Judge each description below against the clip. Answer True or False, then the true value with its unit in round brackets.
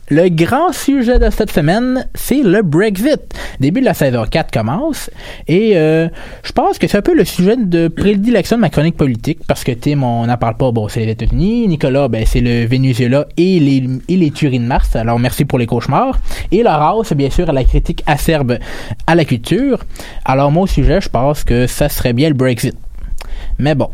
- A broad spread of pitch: True (6.5 semitones)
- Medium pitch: True (150 Hz)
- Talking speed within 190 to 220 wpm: True (210 wpm)